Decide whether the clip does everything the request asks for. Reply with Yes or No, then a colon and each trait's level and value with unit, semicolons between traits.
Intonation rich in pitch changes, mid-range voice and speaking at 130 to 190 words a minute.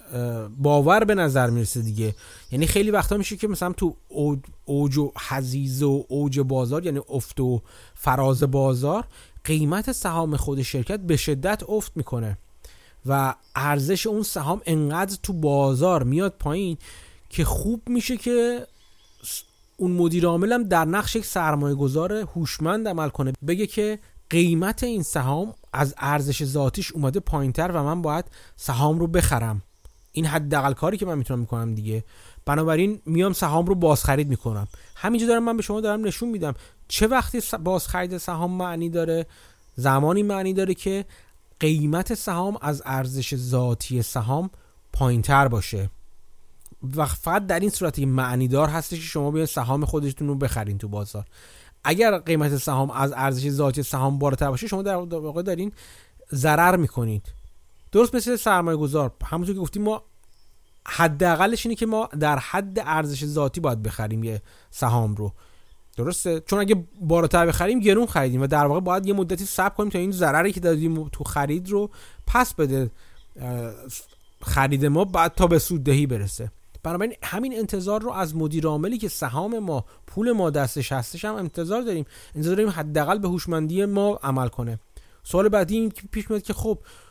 Yes: wide, 6.2 semitones; medium, 155 Hz; fast, 155 wpm